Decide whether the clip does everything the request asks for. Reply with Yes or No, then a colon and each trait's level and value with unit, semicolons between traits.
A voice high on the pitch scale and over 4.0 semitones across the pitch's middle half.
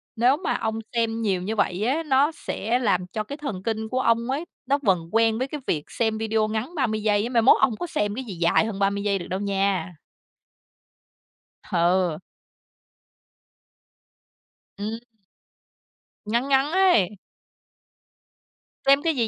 Yes: high, 220 Hz; average, 4.4 semitones